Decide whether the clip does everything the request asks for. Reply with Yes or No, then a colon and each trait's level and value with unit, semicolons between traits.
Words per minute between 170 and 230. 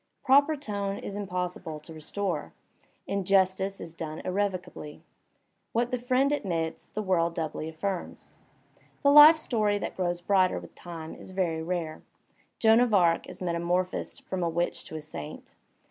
No: average, 150 wpm